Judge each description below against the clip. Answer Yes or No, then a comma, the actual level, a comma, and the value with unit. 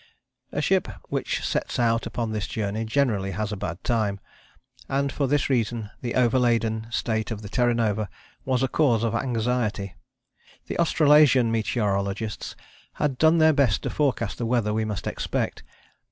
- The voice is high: No, low, 115 Hz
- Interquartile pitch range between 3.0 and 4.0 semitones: Yes, average, 3.3 semitones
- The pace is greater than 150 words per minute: Yes, average, 160 wpm